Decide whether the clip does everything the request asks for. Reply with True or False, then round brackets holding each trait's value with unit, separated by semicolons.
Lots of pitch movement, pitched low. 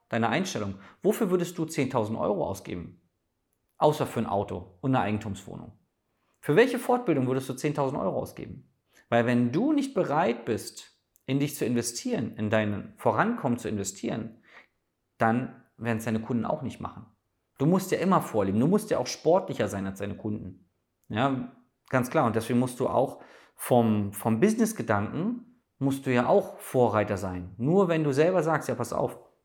True (6.1 semitones; 120 Hz)